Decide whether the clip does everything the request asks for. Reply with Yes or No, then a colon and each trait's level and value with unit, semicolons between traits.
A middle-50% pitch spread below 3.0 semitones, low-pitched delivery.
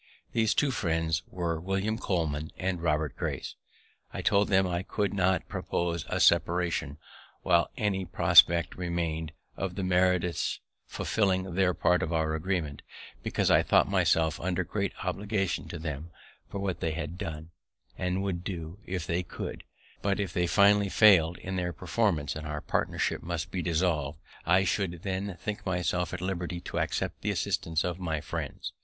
Yes: narrow, 2.6 semitones; very low, 90 Hz